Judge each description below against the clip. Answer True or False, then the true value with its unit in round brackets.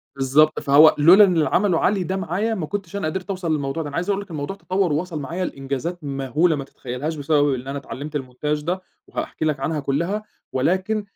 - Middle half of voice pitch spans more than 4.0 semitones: True (4.6 semitones)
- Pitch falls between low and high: True (155 Hz)